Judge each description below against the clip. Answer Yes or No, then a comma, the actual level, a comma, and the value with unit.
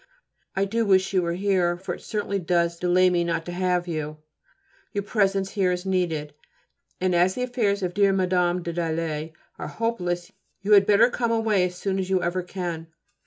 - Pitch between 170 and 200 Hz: Yes, medium, 185 Hz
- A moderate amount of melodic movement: No, narrow, 2.3 semitones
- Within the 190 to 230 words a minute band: Yes, average, 195 wpm